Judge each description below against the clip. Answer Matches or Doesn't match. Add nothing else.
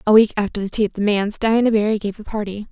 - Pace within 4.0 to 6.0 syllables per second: Doesn't match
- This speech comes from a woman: Matches